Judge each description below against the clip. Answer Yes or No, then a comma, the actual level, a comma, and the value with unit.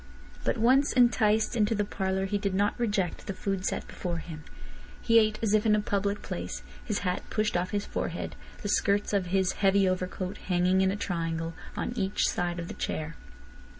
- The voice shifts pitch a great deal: No, narrow, 2.6 semitones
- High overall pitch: Yes, high, 195 Hz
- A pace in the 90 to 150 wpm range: No, average, 195 wpm